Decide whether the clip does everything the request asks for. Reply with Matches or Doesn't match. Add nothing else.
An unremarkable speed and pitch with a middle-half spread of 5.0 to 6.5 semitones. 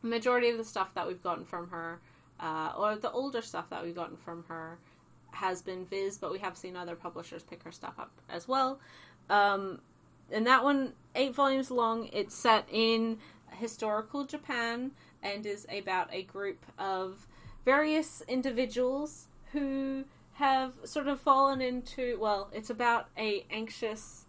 Matches